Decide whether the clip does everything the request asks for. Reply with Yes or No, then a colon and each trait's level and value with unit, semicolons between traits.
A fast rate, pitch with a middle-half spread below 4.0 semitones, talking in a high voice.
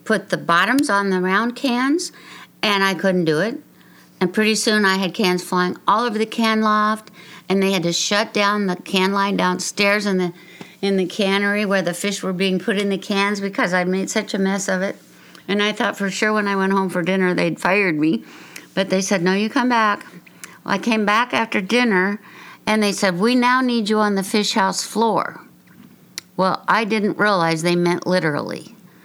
Yes: fast, 210 wpm; narrow, 2.5 semitones; high, 200 Hz